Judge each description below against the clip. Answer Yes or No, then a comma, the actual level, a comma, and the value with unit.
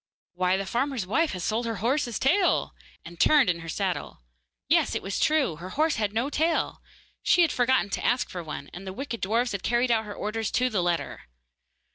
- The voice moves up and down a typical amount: No, wide, 5.8 semitones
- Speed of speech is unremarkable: No, fast, 210 wpm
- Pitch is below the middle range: No, high, 225 Hz